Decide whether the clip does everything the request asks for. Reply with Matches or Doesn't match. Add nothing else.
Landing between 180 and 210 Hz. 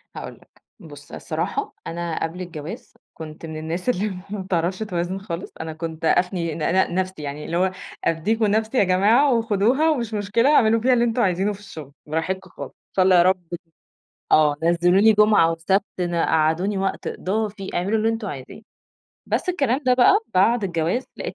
Matches